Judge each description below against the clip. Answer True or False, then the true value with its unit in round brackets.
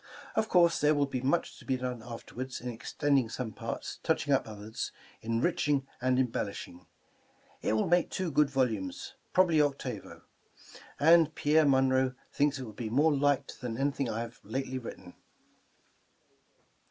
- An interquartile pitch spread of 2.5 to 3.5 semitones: False (4.0 semitones)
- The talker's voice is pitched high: False (130 Hz)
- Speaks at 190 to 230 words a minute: False (165 wpm)